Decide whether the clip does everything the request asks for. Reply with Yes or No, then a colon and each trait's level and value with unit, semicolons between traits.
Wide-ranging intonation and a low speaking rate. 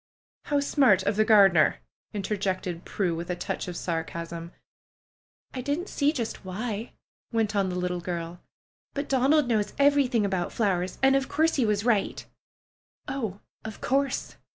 No: wide, 6.7 semitones; average, 155 wpm